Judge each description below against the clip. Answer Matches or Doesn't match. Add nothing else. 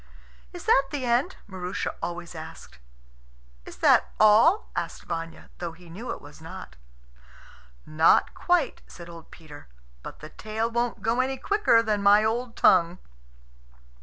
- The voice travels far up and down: Matches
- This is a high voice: Matches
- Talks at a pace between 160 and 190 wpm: Doesn't match